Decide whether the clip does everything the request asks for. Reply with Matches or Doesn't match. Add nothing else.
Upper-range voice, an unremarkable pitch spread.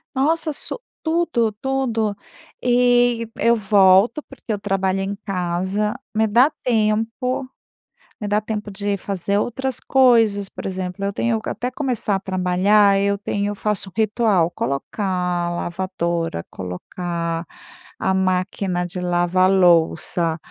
Matches